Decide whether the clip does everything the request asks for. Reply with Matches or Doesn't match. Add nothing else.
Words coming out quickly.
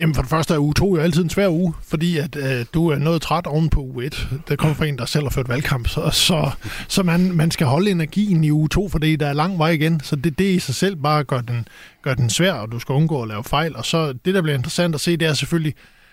Matches